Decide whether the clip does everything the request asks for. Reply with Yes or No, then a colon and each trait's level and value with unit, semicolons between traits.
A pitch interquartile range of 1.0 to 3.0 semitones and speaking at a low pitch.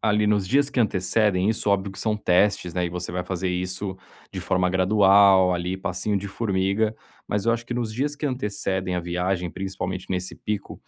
Yes: narrow, 2.6 semitones; very low, 95 Hz